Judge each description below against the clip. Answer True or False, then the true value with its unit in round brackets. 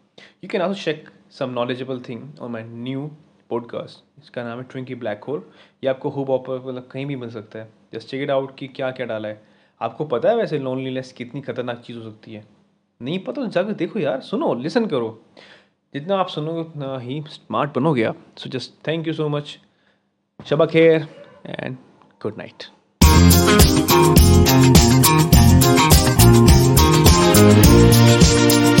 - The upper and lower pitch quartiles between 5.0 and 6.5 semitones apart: False (4.3 semitones)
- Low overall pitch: True (130 Hz)